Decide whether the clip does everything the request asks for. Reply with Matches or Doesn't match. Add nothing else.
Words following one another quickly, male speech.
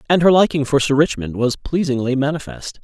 Doesn't match